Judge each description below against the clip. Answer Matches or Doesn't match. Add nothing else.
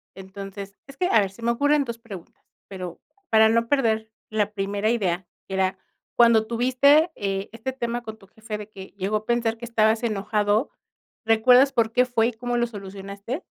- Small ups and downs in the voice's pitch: Doesn't match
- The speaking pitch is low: Doesn't match